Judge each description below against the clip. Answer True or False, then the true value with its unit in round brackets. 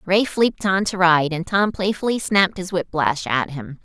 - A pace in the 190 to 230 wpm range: True (205 wpm)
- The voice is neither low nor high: True (180 Hz)